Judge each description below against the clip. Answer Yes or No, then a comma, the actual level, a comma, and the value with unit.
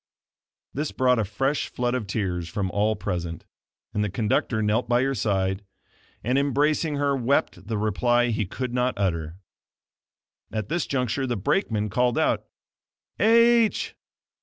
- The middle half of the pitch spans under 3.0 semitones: No, average, 4.6 semitones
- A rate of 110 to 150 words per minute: Yes, average, 145 wpm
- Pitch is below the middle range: Yes, low, 120 Hz